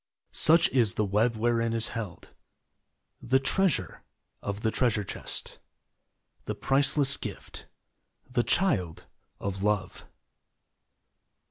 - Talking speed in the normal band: No, slow, 110 wpm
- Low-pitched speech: Yes, low, 115 Hz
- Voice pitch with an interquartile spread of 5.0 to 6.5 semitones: No, average, 4.4 semitones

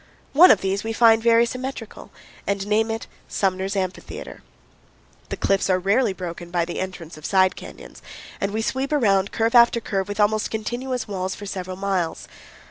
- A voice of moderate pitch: No, high, 200 Hz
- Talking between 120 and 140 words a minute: No, average, 175 wpm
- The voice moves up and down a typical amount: Yes, average, 3.2 semitones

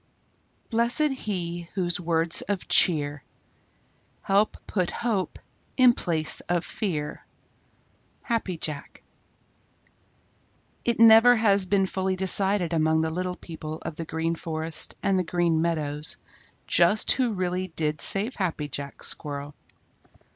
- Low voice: No, medium, 175 Hz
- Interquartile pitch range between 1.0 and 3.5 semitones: No, average, 4.0 semitones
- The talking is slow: Yes, slow, 120 wpm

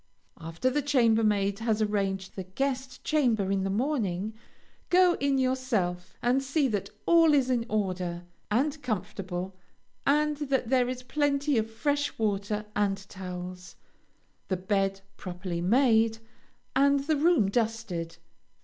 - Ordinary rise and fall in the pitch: No, wide, 5.8 semitones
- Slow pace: Yes, slow, 130 wpm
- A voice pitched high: Yes, high, 220 Hz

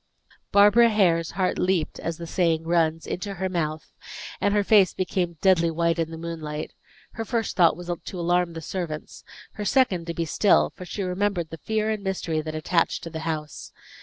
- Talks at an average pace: Yes, average, 190 wpm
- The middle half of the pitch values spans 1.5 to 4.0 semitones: Yes, average, 3.1 semitones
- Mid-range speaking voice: Yes, medium, 175 Hz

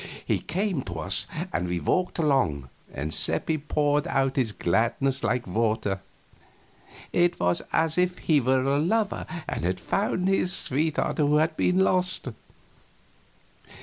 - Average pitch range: No, wide, 7.6 semitones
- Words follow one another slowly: No, average, 150 wpm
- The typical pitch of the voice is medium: Yes, medium, 145 Hz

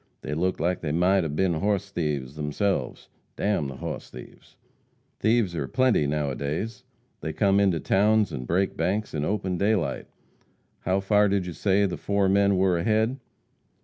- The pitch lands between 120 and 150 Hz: No, very low, 95 Hz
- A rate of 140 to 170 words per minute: No, average, 180 wpm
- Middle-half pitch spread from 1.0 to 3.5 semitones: No, average, 4.4 semitones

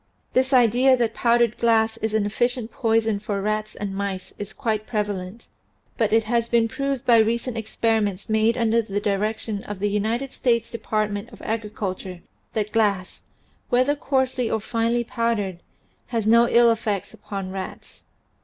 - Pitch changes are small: Yes, narrow, 2.2 semitones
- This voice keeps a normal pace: Yes, average, 155 wpm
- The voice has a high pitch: Yes, high, 220 Hz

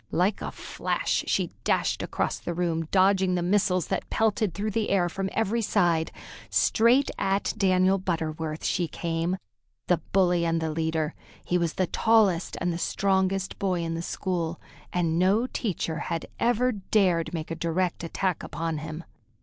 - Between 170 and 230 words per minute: No, average, 160 wpm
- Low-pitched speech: No, medium, 180 Hz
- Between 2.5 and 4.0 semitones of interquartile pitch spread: Yes, average, 2.9 semitones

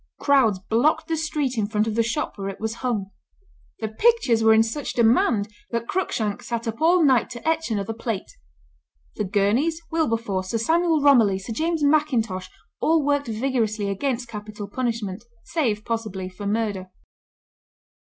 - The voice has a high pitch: Yes, high, 230 Hz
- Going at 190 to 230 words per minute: No, average, 160 wpm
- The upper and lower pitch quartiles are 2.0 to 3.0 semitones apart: No, average, 5.3 semitones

